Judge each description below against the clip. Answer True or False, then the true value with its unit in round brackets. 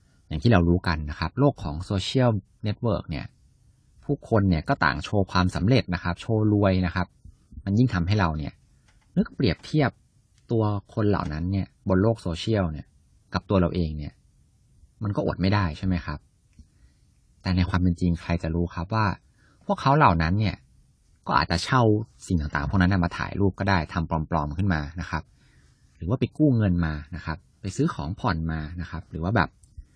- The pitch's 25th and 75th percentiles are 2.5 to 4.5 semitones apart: True (4.0 semitones)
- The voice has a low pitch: True (90 Hz)